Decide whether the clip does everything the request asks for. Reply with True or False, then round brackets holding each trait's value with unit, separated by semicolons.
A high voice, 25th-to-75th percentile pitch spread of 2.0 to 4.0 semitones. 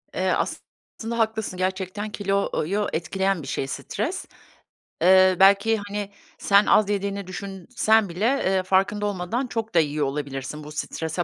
True (195 Hz; 2.7 semitones)